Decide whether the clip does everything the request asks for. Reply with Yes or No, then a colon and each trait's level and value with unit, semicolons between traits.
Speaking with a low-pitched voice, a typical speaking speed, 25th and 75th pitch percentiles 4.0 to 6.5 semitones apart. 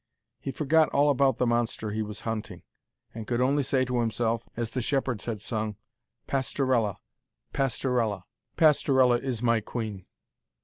No: low, 120 Hz; average, 145 wpm; average, 3.3 semitones